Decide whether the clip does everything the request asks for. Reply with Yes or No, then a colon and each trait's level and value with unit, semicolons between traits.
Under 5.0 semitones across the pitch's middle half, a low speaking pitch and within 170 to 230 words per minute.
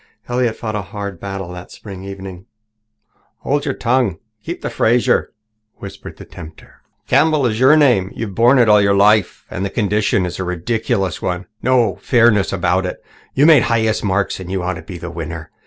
Yes: average, 4.1 semitones; low, 100 Hz; average, 200 wpm